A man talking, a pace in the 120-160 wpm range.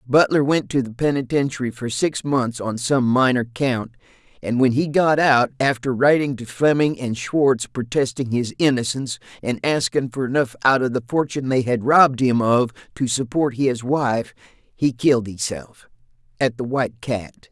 No: male; average, 170 wpm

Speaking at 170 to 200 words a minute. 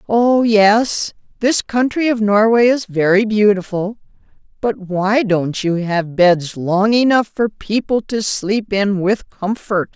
No: average, 145 wpm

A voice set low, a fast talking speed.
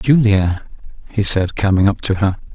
No: low, 100 Hz; average, 165 wpm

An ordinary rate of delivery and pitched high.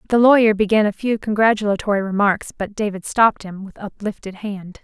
Yes: average, 175 wpm; high, 205 Hz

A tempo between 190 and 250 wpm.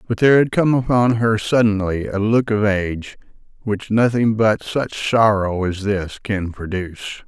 No: average, 165 wpm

